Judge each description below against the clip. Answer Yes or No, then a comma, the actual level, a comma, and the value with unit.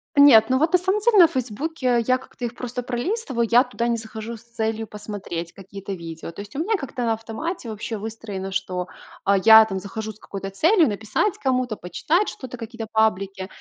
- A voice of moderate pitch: No, high, 225 Hz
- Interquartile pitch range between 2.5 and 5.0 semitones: Yes, average, 4.0 semitones